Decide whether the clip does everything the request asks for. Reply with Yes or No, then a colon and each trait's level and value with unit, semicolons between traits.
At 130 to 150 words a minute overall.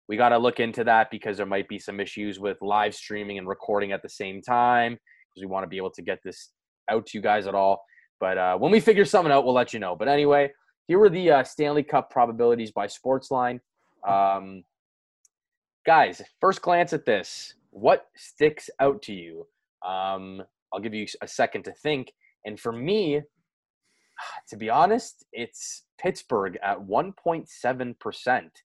No: average, 180 wpm